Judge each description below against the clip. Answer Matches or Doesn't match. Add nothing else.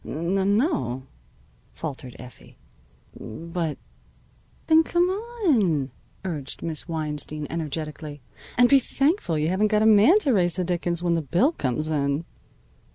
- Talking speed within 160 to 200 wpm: Doesn't match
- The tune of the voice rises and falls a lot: Matches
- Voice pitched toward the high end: Doesn't match